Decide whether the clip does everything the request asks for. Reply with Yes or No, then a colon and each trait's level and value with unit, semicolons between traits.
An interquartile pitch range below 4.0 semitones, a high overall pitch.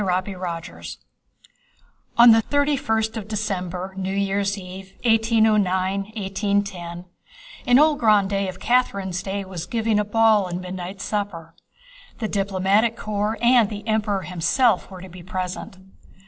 Yes: average, 2.9 semitones; high, 200 Hz